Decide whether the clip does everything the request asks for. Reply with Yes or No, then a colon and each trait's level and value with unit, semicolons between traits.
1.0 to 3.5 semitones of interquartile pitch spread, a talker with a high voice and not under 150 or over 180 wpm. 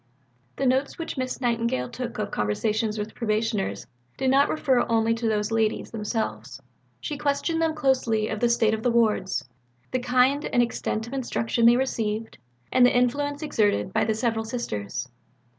Yes: average, 3.0 semitones; high, 230 Hz; average, 170 wpm